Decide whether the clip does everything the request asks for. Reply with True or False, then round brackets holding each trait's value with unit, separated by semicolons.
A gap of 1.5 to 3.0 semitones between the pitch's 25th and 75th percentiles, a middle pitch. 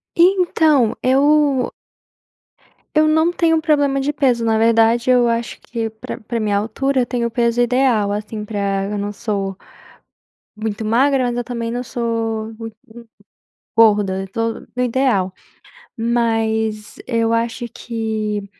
False (2.7 semitones; 230 Hz)